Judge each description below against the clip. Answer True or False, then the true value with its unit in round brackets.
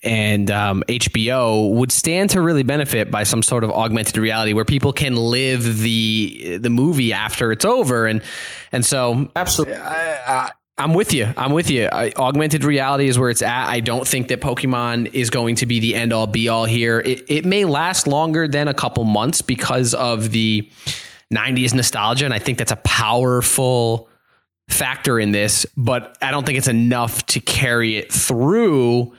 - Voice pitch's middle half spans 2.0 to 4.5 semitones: True (2.8 semitones)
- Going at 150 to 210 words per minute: True (185 wpm)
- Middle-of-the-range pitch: False (120 Hz)